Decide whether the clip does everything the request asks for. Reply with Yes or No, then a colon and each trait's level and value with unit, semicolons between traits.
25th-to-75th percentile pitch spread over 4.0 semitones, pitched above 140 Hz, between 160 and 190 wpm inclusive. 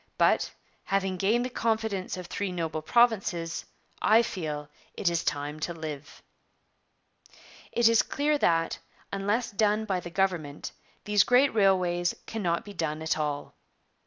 No: average, 4.8 semitones; medium, 185 Hz; average, 140 wpm